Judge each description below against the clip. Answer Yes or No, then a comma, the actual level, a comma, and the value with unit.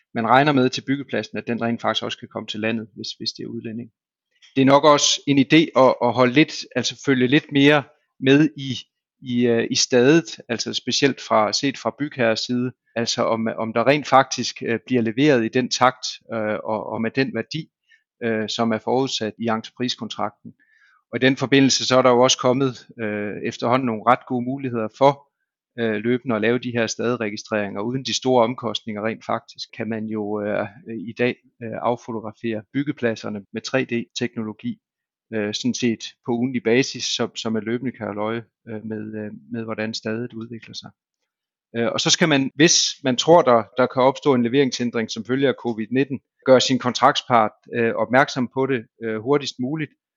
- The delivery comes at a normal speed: Yes, average, 180 wpm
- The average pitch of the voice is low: Yes, low, 120 Hz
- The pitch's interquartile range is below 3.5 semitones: Yes, average, 2.8 semitones